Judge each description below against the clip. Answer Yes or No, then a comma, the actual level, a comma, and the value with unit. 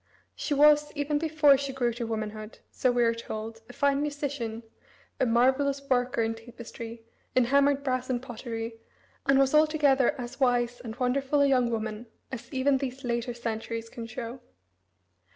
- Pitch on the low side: No, very high, 250 Hz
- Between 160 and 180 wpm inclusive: Yes, average, 165 wpm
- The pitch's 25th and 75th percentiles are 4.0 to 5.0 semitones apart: No, average, 3.2 semitones